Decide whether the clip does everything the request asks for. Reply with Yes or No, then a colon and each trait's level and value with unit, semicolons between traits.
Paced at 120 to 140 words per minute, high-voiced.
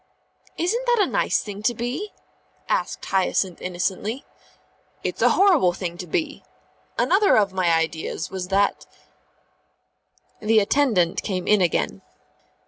Yes: slow, 135 wpm; high, 200 Hz